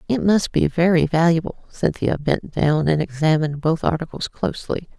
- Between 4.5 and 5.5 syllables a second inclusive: Yes, 5.2 syllables/s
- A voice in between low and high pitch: Yes, medium, 150 Hz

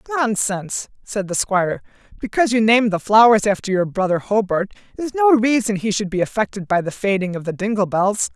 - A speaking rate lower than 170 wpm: No, average, 195 wpm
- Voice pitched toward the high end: Yes, high, 210 Hz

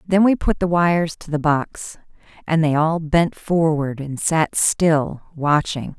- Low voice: No, medium, 160 Hz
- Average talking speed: Yes, average, 170 wpm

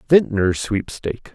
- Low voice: Yes, low, 115 Hz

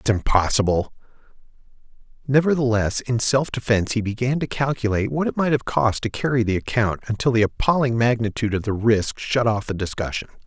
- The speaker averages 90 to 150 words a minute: No, average, 170 wpm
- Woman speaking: No, male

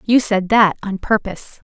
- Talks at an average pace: Yes, average, 175 wpm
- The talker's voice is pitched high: Yes, high, 205 Hz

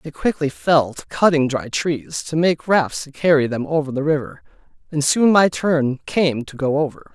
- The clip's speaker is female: No, male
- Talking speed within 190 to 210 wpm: Yes, average, 200 wpm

